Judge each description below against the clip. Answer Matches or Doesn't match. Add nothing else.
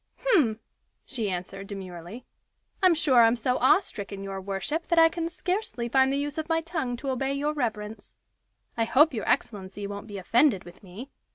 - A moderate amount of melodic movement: Doesn't match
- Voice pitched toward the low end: Doesn't match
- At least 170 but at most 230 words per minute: Matches